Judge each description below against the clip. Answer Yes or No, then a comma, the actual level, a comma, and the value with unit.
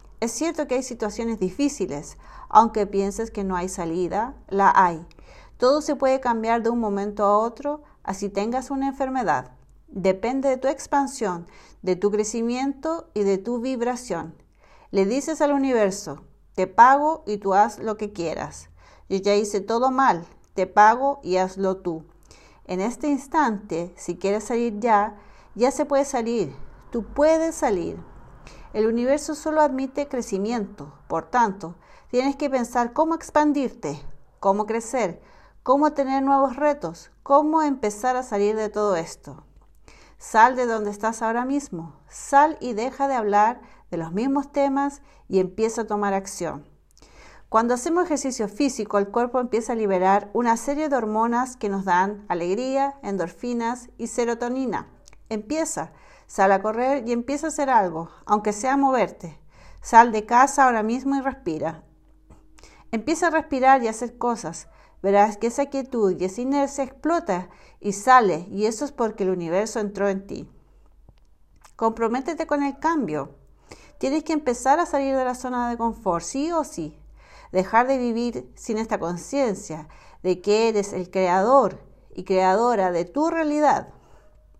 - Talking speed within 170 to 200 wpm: No, average, 155 wpm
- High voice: Yes, high, 230 Hz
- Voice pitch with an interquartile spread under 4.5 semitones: No, wide, 5.6 semitones